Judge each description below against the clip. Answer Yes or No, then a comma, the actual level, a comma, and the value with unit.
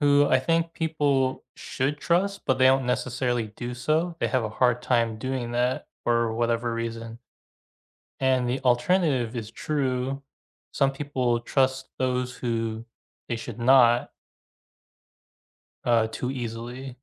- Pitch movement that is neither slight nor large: No, narrow, 2.3 semitones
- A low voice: Yes, low, 125 Hz